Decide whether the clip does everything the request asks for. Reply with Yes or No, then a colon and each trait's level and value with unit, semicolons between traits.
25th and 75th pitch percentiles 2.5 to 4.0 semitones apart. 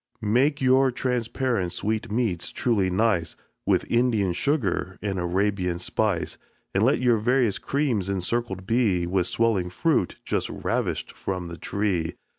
No: average, 4.9 semitones